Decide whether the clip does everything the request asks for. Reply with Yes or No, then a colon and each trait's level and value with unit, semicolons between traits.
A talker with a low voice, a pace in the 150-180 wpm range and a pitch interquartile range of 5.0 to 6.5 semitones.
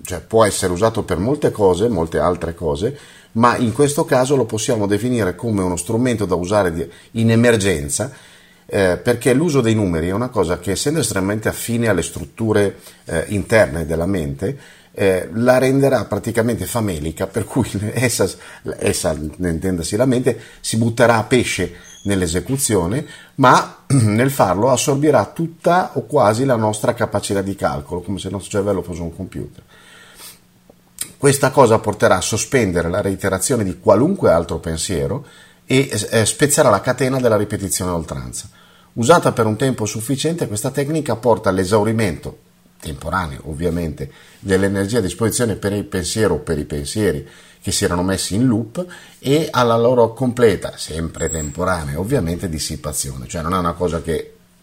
Yes: low, 105 Hz; average, 155 wpm; wide, 5.5 semitones